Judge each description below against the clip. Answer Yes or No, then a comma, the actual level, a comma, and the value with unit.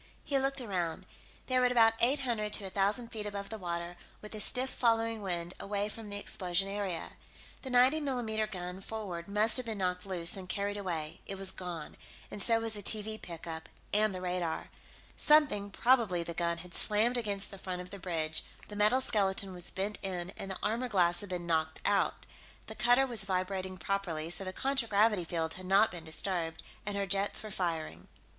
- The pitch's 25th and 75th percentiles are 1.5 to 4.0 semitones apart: Yes, average, 3.6 semitones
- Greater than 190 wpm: Yes, average, 200 wpm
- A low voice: No, high, 200 Hz